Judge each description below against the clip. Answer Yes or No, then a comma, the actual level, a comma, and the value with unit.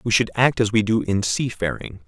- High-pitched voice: No, low, 105 Hz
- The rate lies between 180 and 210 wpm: No, fast, 230 wpm